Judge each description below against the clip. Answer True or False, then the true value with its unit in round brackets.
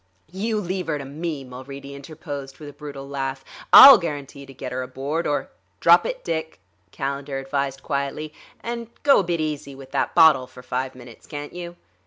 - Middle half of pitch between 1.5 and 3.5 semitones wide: True (3.1 semitones)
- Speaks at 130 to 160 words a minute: False (185 wpm)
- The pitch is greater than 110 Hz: True (140 Hz)